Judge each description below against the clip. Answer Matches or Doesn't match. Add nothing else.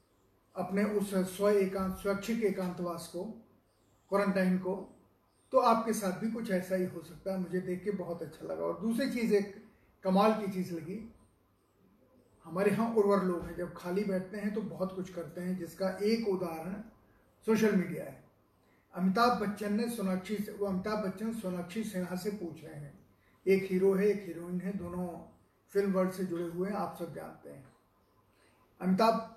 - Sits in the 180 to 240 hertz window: Matches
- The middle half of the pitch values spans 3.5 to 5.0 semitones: Doesn't match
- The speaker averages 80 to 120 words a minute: Doesn't match